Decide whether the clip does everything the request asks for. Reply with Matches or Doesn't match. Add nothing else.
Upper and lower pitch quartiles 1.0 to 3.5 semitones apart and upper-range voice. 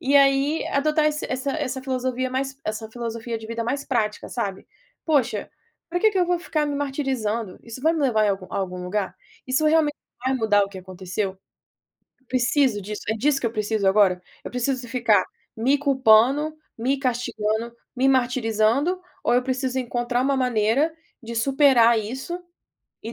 Doesn't match